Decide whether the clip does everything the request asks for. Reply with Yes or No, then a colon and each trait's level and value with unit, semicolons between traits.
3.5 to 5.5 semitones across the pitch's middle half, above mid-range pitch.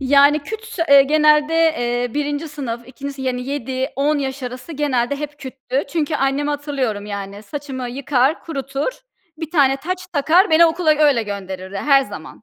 No: average, 3.0 semitones; very high, 280 Hz